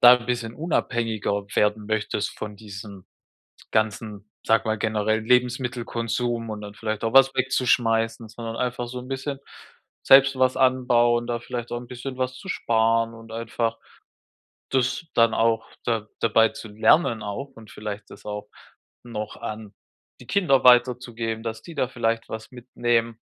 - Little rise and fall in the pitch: Yes, narrow, 2.1 semitones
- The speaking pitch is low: Yes, low, 115 Hz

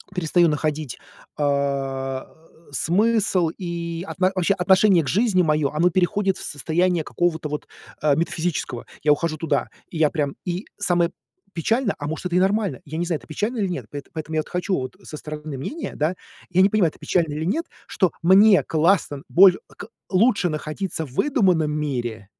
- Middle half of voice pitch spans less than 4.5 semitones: Yes, average, 3.7 semitones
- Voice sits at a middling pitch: Yes, medium, 170 Hz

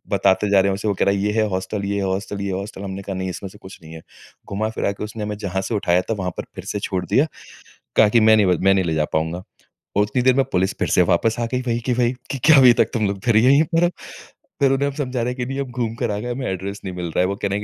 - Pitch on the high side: No, low, 105 Hz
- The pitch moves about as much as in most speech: Yes, average, 3.8 semitones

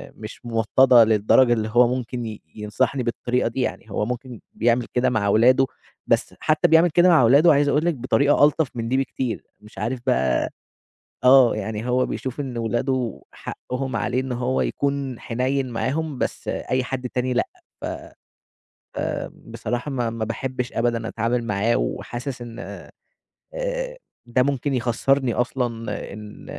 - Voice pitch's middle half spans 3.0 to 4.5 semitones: No, narrow, 2.6 semitones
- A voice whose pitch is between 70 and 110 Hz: No, low, 125 Hz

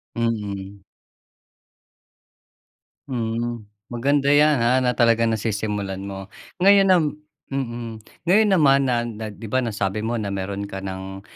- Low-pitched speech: Yes, low, 115 Hz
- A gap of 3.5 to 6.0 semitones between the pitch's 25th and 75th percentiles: Yes, average, 4.2 semitones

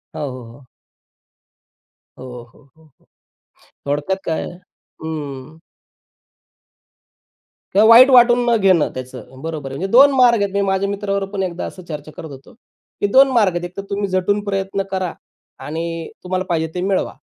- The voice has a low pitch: No, medium, 185 Hz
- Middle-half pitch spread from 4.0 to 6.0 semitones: Yes, average, 4.5 semitones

